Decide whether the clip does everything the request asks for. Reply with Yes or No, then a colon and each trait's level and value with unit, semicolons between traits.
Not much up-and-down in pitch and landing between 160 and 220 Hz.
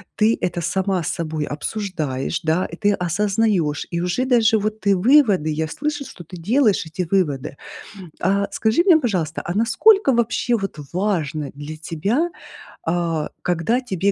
No: wide, 5.4 semitones; high, 190 Hz